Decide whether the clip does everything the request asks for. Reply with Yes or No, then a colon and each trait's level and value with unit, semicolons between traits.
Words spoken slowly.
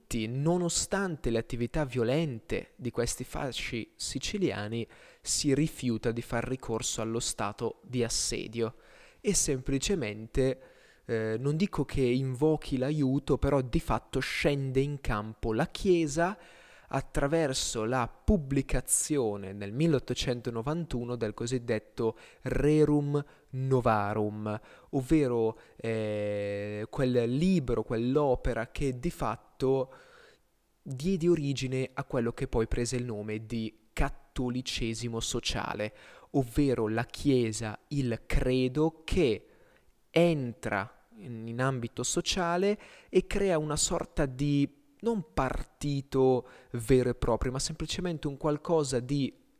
Yes: slow, 105 wpm